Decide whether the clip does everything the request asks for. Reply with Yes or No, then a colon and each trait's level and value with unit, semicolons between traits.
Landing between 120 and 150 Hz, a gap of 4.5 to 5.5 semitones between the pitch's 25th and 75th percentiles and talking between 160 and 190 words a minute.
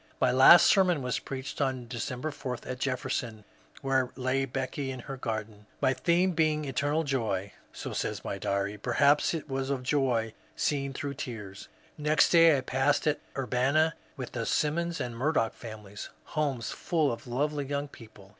No: low, 135 Hz; average, 3.4 semitones; average, 170 wpm